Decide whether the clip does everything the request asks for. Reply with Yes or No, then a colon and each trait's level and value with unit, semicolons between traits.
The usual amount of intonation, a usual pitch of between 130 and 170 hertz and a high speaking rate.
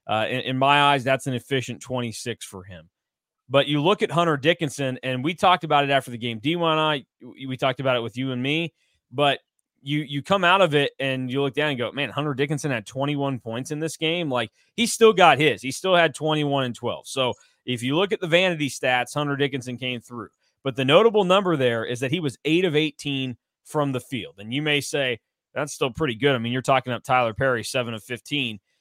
Yes: average, 3.3 semitones; medium, 140 Hz; fast, 235 wpm